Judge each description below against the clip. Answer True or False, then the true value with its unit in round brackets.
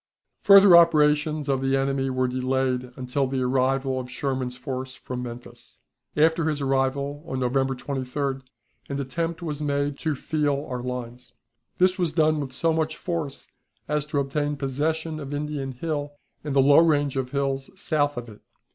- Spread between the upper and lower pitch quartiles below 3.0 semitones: True (2.4 semitones)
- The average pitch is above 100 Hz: True (140 Hz)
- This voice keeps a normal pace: True (165 wpm)